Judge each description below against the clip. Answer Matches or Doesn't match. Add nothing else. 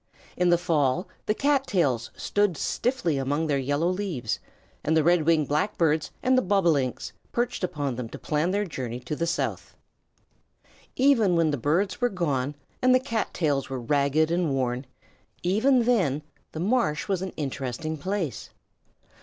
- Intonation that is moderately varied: Doesn't match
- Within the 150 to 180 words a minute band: Matches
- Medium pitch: Matches